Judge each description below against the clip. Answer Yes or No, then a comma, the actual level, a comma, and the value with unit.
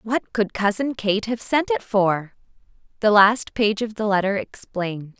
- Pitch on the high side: Yes, high, 210 Hz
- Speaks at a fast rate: No, average, 175 wpm